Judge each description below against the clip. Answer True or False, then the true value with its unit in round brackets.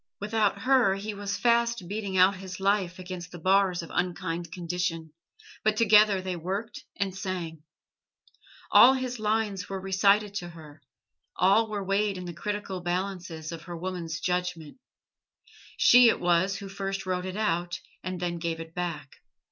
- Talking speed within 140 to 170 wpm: True (160 wpm)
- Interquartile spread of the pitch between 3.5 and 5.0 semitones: False (2.7 semitones)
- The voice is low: False (185 Hz)